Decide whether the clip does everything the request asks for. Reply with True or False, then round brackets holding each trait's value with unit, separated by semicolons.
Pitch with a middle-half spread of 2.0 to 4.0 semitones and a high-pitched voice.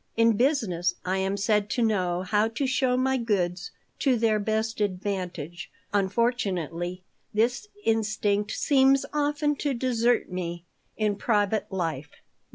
False (4.7 semitones; 210 Hz)